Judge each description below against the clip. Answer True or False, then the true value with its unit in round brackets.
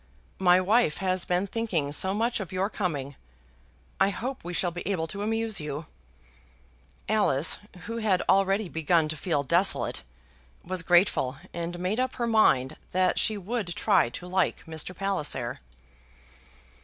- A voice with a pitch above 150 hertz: True (185 Hz)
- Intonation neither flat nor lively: True (4.0 semitones)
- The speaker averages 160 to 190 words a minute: False (150 wpm)